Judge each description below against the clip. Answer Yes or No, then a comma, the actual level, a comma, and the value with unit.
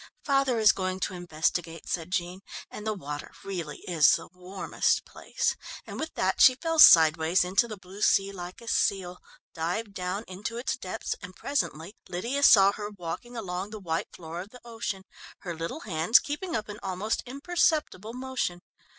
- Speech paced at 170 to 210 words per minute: Yes, average, 175 wpm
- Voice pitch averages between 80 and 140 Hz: No, high, 190 Hz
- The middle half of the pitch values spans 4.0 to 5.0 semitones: Yes, average, 4.5 semitones